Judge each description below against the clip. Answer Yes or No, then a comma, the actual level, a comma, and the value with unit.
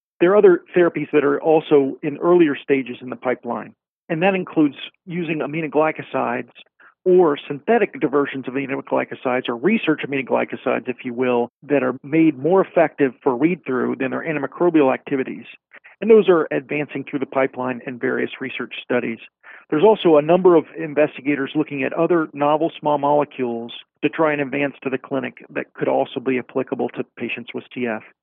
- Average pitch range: Yes, average, 3.4 semitones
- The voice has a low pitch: No, medium, 145 Hz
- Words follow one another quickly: No, average, 170 wpm